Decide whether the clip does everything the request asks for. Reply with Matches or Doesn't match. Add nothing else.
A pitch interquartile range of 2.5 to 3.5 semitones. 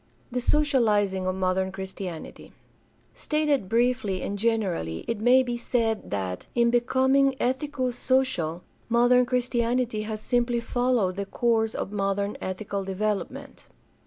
Doesn't match